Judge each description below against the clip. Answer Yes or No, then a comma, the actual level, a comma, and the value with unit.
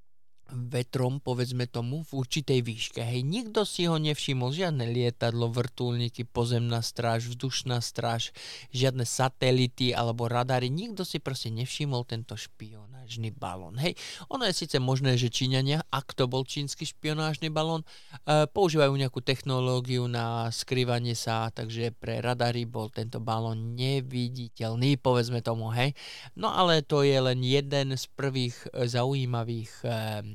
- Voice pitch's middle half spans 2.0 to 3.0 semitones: Yes, average, 2.7 semitones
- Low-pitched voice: Yes, low, 125 Hz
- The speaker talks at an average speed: Yes, average, 135 wpm